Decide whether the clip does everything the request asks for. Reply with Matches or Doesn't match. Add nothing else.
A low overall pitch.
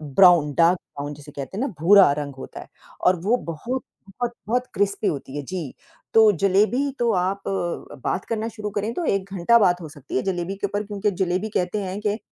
Doesn't match